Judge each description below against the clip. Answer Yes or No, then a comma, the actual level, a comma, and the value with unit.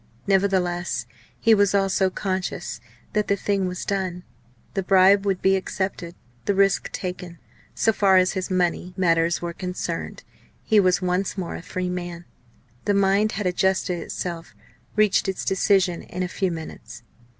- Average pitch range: No, narrow, 1.6 semitones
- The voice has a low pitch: No, medium, 185 Hz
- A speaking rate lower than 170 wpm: Yes, average, 155 wpm